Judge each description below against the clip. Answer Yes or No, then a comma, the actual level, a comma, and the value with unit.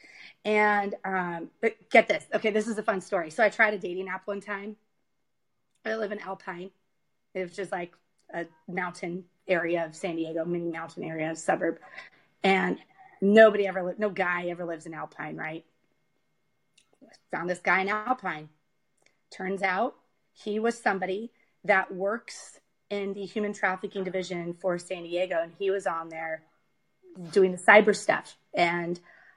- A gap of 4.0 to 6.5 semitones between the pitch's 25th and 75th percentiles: No, average, 3.2 semitones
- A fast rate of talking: No, average, 160 wpm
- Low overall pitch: No, high, 190 Hz